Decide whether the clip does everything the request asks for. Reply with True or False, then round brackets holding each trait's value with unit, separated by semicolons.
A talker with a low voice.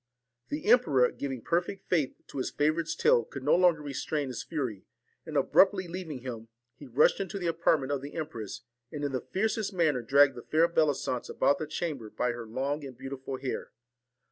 False (145 Hz)